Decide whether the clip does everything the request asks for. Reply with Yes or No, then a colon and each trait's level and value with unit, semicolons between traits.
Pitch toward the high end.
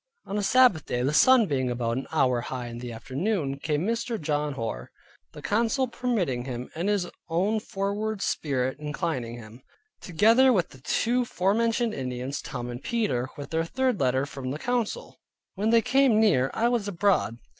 No: medium, 165 Hz